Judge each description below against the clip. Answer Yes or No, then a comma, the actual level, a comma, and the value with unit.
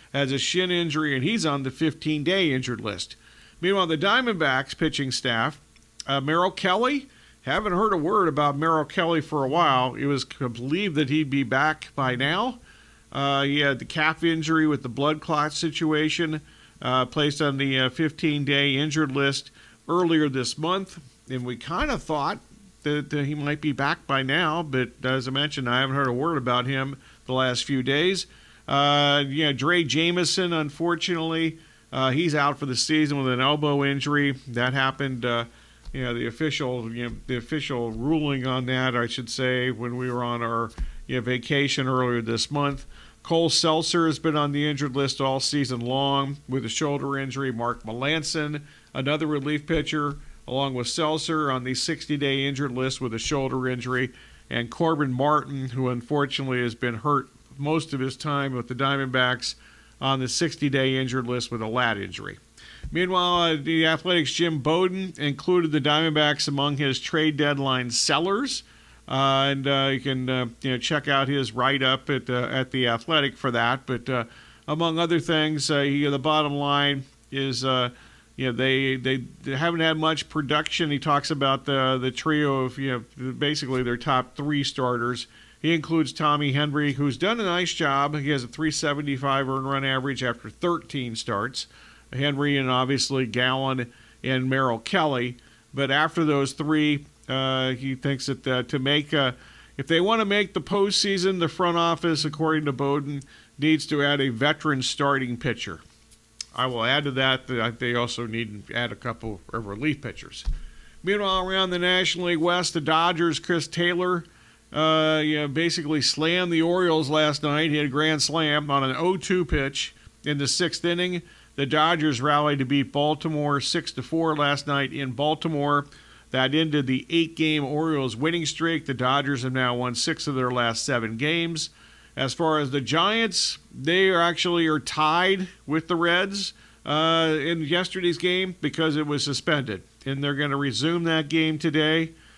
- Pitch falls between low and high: Yes, medium, 145 Hz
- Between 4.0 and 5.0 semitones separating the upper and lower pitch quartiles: No, average, 3.4 semitones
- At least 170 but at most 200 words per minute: Yes, average, 175 wpm